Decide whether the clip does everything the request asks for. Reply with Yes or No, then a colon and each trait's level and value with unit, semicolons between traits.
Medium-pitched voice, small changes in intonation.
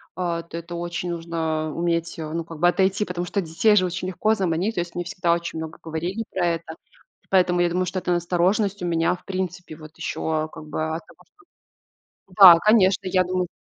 Yes: medium, 175 Hz; narrow, 1.9 semitones